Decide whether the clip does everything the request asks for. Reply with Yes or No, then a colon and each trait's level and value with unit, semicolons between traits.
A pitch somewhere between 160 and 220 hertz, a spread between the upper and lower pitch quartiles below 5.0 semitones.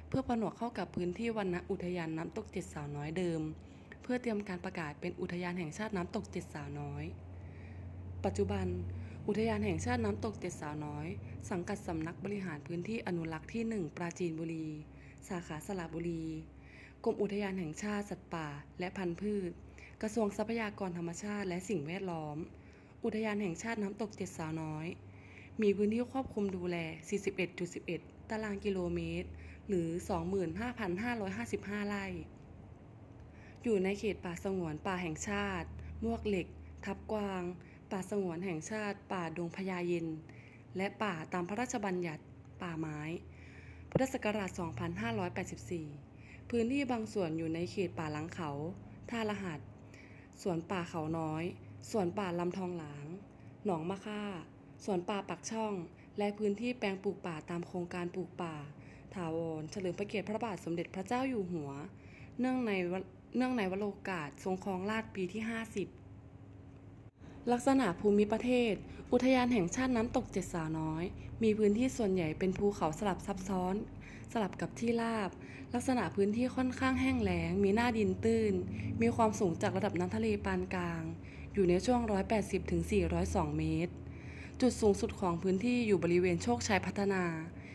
Yes: medium, 185 Hz; average, 4.3 semitones